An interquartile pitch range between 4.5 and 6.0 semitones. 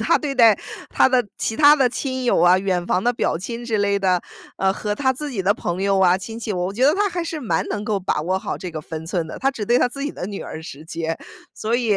Yes: wide, 5.4 semitones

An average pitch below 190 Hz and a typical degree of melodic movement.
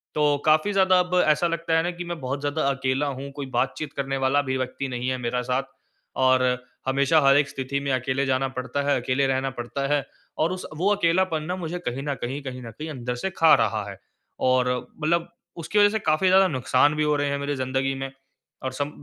Yes: medium, 140 Hz; average, 3.5 semitones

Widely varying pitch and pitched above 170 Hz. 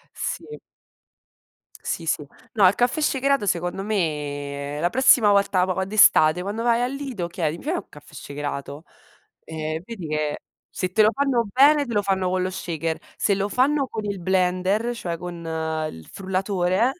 Yes: wide, 5.7 semitones; high, 190 Hz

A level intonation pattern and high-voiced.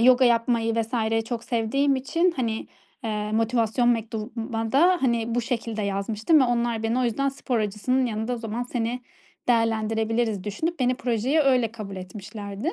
Yes: narrow, 2.2 semitones; high, 230 Hz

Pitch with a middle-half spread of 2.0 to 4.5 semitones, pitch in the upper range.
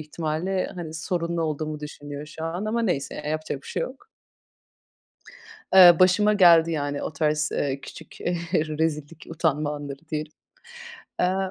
No: average, 2.8 semitones; medium, 160 Hz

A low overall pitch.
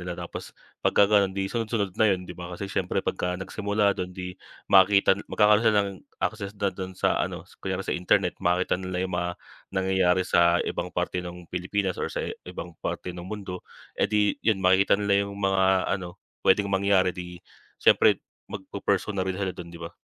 Yes: very low, 95 Hz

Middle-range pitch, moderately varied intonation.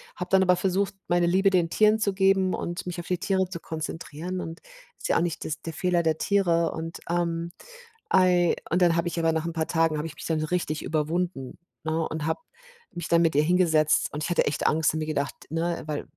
No: medium, 170 Hz; narrow, 2.2 semitones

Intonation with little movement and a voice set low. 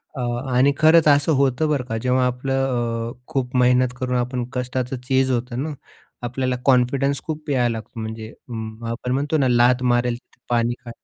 Yes: narrow, 1.8 semitones; low, 125 Hz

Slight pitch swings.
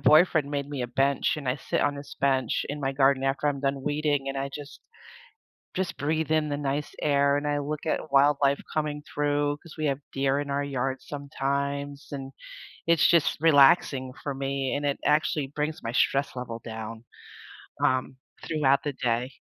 Yes: narrow, 1.5 semitones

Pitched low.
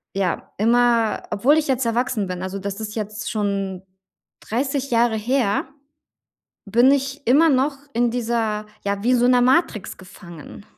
No: high, 230 Hz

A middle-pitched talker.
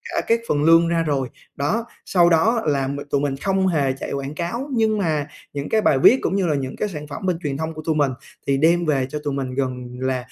Yes: medium, 150 Hz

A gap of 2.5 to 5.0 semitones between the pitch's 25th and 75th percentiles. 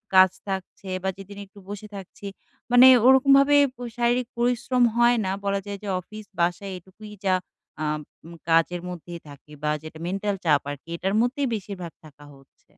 No: wide, 5.5 semitones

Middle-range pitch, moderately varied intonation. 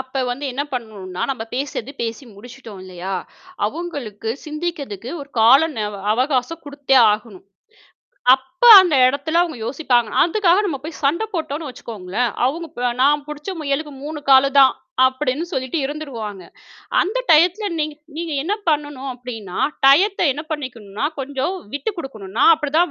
No: very high, 275 Hz; average, 4.3 semitones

